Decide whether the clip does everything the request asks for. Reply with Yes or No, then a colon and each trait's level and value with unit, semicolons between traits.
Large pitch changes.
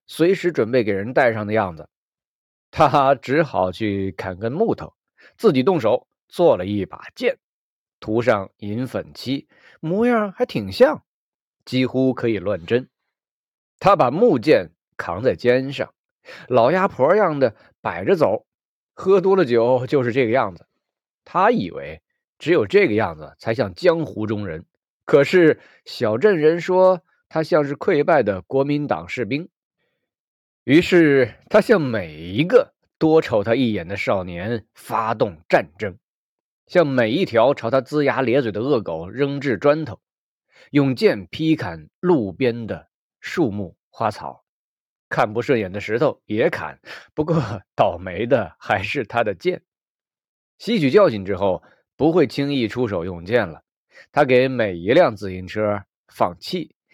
Yes: wide, 6.8 semitones